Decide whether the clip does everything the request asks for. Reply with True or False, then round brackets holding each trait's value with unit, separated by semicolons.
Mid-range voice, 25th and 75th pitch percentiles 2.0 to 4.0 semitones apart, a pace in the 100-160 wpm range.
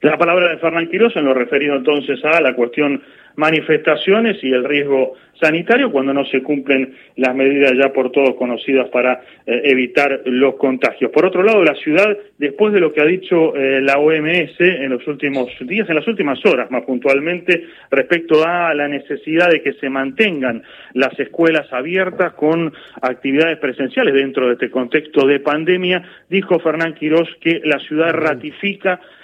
False (150 Hz; 3.7 semitones; 170 wpm)